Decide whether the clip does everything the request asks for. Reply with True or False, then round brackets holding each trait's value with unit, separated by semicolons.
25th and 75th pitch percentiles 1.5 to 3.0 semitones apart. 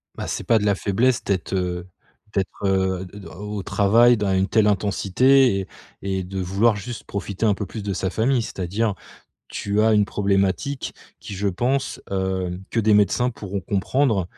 True (2.7 semitones)